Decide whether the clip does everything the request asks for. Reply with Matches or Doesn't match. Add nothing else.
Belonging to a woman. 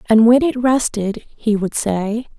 Matches